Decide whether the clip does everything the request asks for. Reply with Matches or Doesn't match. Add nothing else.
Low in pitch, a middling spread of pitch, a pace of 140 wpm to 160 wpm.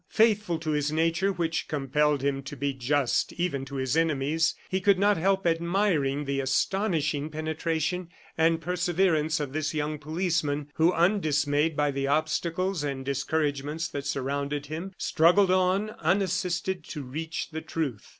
Doesn't match